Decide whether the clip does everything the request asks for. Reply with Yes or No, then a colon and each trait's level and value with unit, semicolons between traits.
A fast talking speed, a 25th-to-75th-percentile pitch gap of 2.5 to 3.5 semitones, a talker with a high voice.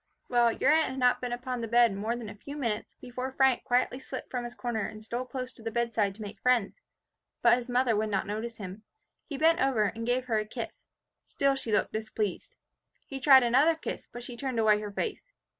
Yes: fast, 225 wpm; average, 3.1 semitones; high, 240 Hz